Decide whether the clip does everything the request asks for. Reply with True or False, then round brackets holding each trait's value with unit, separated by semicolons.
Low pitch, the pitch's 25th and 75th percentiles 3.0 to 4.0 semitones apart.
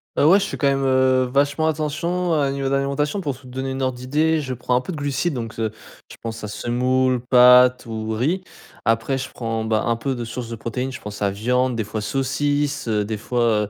True (130 Hz; 3.5 semitones)